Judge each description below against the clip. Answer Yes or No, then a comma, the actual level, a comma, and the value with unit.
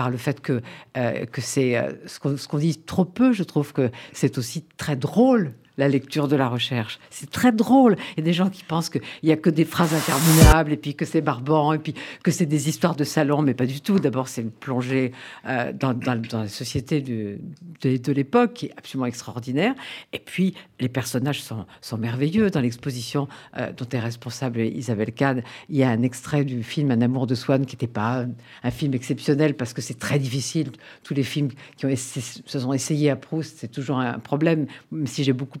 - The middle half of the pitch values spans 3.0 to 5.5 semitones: Yes, average, 3.6 semitones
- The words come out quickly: Yes, fast, 230 wpm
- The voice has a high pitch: No, medium, 140 Hz